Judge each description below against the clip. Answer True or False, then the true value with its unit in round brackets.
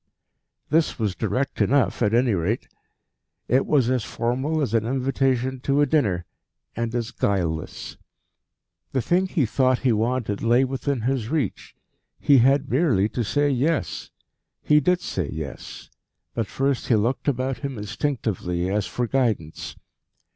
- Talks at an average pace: True (145 wpm)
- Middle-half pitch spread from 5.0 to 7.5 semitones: False (4.0 semitones)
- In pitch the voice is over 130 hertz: False (125 Hz)